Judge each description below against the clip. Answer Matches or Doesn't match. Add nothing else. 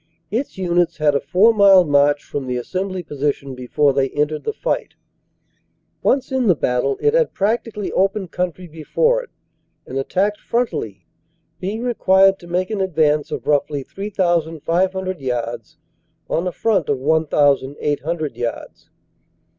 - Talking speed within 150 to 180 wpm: Doesn't match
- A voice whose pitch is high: Doesn't match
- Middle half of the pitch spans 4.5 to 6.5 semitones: Matches